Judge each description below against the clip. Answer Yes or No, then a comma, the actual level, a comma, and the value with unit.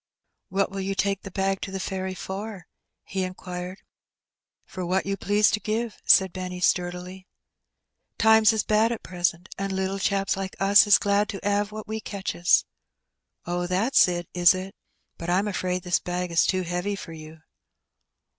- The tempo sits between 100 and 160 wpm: No, average, 175 wpm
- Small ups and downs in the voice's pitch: Yes, narrow, 2.0 semitones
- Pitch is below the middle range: No, high, 190 Hz